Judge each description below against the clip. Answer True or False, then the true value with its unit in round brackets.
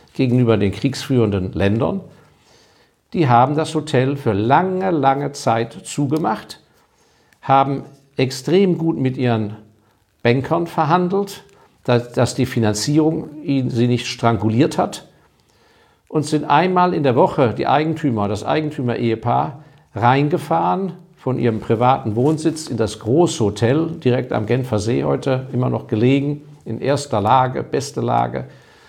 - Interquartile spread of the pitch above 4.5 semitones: True (5.0 semitones)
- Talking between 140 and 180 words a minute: False (125 wpm)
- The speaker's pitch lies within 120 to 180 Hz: True (135 Hz)